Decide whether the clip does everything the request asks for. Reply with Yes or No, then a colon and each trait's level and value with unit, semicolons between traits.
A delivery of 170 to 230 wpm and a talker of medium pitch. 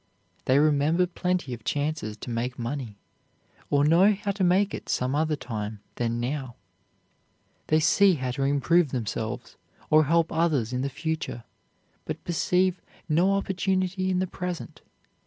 No: average, 150 wpm; medium, 155 Hz